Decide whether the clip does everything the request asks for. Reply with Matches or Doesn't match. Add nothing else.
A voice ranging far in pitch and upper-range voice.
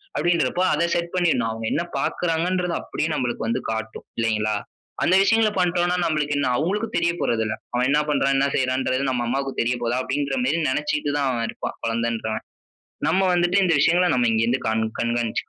Doesn't match